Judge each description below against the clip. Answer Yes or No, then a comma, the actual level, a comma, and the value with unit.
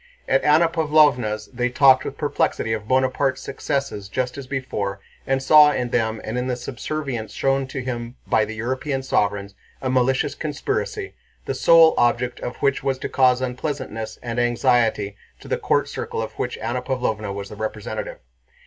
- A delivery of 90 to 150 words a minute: No, average, 170 wpm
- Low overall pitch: Yes, low, 125 Hz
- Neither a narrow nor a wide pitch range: Yes, average, 3.5 semitones